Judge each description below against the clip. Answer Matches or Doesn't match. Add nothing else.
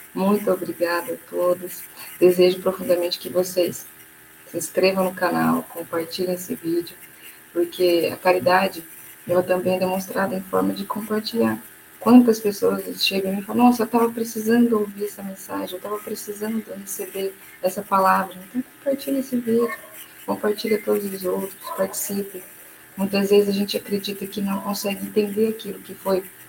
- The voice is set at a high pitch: Matches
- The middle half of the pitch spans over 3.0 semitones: Doesn't match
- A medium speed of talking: Matches